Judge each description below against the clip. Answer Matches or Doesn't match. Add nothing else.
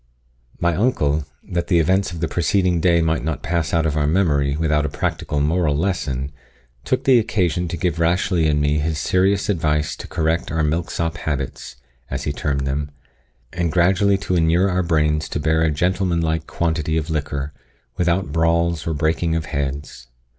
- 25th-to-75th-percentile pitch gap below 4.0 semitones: Matches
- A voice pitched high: Doesn't match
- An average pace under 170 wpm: Doesn't match